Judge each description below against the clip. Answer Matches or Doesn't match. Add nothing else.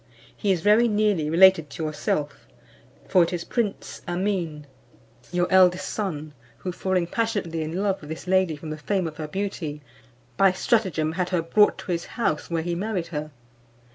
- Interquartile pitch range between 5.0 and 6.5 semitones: Doesn't match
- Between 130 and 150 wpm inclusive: Doesn't match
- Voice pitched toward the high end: Doesn't match